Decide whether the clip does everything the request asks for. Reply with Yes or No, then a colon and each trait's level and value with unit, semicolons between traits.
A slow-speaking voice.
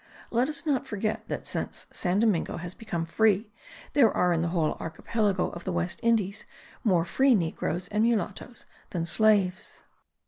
No: average, 165 wpm